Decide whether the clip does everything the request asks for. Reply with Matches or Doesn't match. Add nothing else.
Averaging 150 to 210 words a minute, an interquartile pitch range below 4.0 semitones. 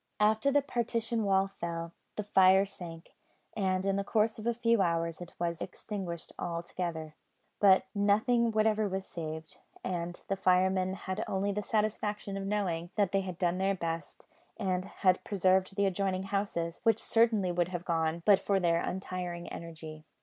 Matches